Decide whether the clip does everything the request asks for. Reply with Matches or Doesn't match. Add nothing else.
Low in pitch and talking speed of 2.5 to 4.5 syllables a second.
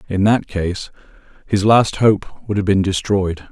Matches